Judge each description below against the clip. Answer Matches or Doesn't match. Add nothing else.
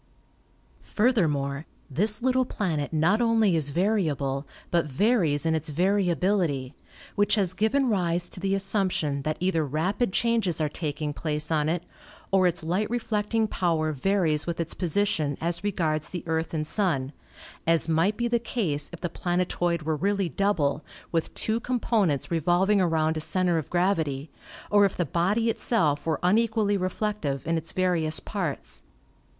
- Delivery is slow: Doesn't match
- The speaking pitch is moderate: Matches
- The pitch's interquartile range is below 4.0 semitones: Doesn't match